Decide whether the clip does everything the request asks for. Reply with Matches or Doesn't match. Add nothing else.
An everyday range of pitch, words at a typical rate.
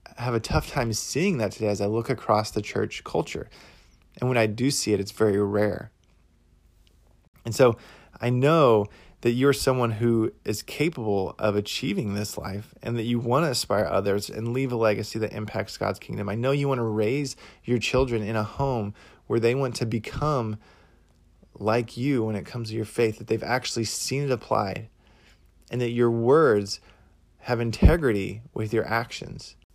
Matches